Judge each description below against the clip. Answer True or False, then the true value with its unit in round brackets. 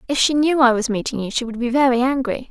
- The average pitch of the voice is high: True (250 Hz)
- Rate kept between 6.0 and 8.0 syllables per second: True (6.4 syllables/s)